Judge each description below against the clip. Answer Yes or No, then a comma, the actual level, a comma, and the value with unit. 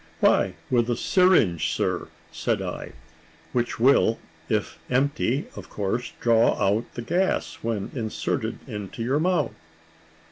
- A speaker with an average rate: No, slow, 130 wpm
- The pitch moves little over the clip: No, average, 4.1 semitones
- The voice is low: Yes, low, 120 Hz